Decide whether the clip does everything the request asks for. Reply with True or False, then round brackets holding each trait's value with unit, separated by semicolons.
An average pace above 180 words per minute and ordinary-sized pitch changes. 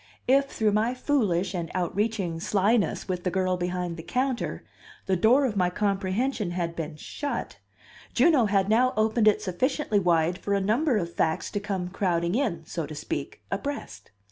False (170 wpm; 4.3 semitones)